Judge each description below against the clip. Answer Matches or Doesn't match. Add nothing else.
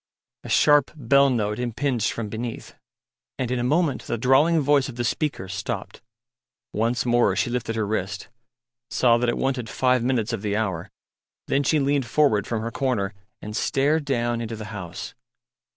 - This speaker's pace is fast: Doesn't match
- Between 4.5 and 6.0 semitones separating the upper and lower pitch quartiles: Doesn't match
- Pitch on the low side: Matches